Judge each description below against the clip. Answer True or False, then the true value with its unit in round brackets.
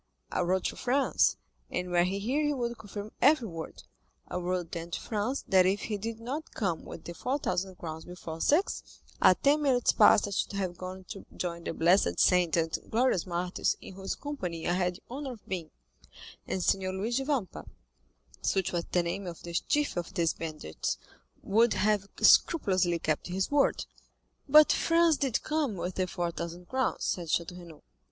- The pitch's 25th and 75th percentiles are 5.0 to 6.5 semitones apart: True (5.5 semitones)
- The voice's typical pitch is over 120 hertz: True (190 Hz)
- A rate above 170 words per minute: True (185 wpm)